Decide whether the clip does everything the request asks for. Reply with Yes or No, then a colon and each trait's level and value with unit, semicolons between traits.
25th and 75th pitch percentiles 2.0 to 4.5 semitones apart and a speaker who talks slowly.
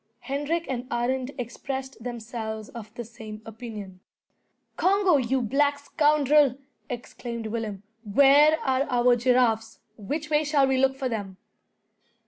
Yes: average, 3.9 semitones; slow, 125 wpm